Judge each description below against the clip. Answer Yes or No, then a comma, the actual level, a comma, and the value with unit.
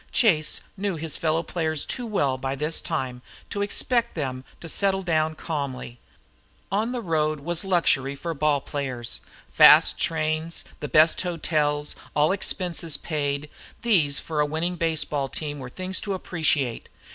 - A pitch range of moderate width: Yes, average, 3.4 semitones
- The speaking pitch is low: No, medium, 155 Hz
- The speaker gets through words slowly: No, average, 150 wpm